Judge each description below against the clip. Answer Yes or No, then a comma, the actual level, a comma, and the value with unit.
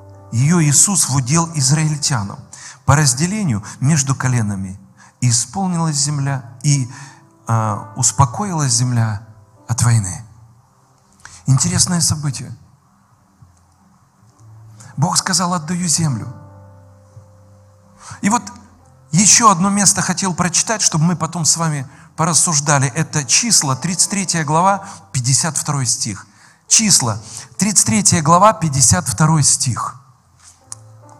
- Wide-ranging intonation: Yes, wide, 6.8 semitones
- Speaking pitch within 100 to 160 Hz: Yes, medium, 140 Hz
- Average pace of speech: No, slow, 90 wpm